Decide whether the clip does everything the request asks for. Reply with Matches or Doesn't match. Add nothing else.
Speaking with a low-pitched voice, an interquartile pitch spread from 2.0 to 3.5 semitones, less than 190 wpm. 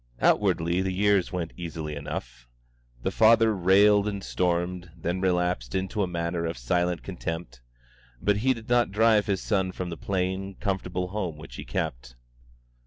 Matches